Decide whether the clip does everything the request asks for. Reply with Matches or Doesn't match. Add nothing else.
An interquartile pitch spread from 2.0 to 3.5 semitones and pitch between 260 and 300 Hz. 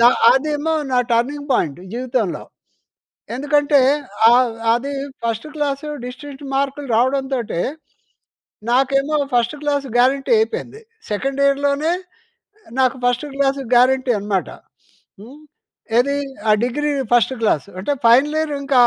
Matches